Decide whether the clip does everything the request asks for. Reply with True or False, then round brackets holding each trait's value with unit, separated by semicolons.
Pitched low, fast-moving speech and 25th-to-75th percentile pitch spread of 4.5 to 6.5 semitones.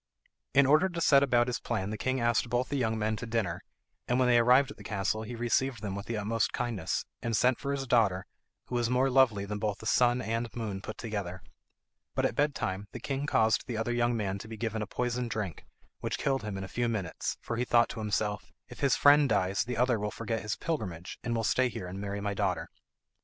False (115 Hz; 245 wpm; 3.2 semitones)